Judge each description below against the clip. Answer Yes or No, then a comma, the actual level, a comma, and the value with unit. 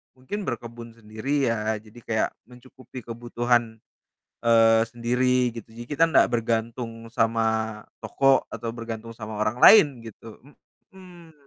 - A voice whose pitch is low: Yes, low, 115 Hz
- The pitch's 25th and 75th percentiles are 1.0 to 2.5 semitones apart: Yes, narrow, 2.0 semitones